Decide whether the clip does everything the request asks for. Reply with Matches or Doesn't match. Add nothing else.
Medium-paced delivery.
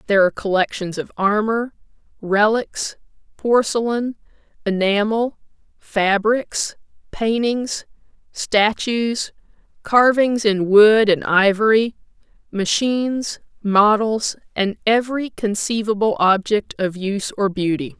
Doesn't match